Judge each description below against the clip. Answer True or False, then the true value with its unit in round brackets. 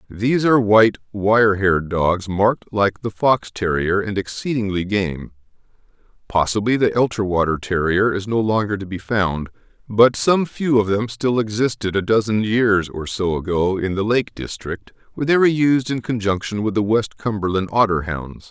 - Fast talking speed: False (170 wpm)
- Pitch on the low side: True (105 Hz)